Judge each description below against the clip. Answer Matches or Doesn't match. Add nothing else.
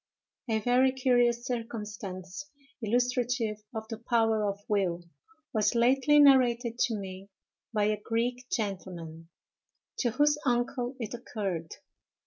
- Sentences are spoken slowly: Matches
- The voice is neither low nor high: Doesn't match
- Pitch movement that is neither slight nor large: Matches